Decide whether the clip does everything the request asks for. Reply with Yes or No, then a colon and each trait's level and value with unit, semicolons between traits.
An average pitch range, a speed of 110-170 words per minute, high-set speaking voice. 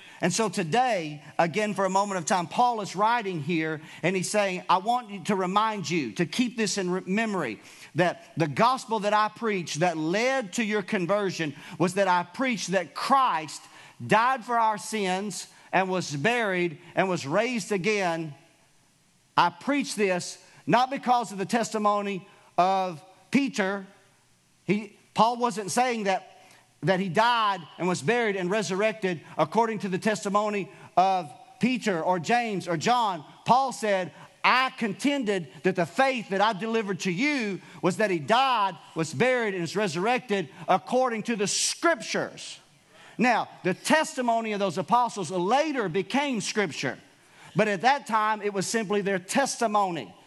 Yes: average, 3.9 semitones; average, 155 wpm; high, 200 Hz